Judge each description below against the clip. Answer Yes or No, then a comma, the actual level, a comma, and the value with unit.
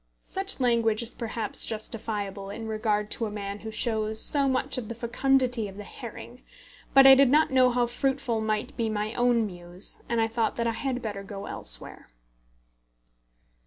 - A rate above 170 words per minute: Yes, average, 180 wpm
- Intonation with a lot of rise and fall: No, average, 2.8 semitones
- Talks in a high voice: Yes, high, 225 Hz